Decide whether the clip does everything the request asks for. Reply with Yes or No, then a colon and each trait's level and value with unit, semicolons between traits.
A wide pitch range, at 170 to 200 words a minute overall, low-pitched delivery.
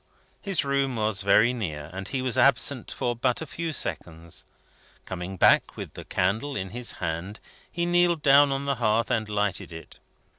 Yes: wide, 6.5 semitones; average, 180 wpm; low, 115 Hz